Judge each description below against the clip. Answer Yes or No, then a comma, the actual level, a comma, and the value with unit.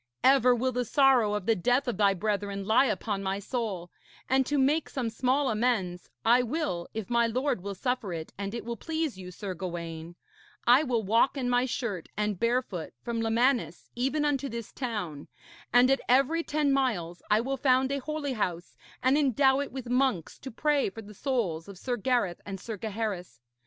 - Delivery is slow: No, average, 195 wpm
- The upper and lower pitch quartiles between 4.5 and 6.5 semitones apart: Yes, average, 5.0 semitones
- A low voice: No, high, 235 Hz